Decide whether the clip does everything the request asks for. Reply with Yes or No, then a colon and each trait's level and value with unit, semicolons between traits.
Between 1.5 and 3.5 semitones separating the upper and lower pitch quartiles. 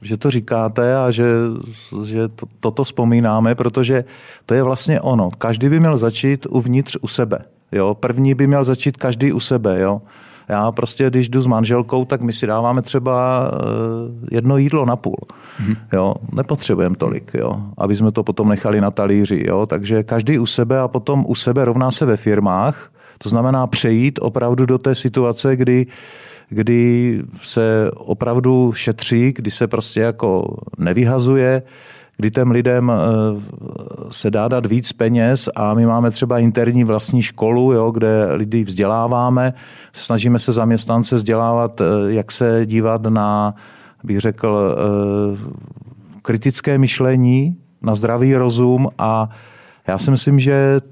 Yes: narrow, 2.6 semitones